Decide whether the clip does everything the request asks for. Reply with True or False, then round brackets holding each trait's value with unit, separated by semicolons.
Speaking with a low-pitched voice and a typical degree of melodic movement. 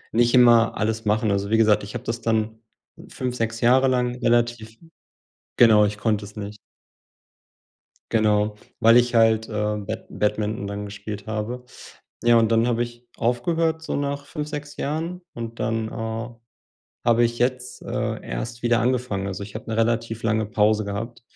False (115 Hz; 2.2 semitones)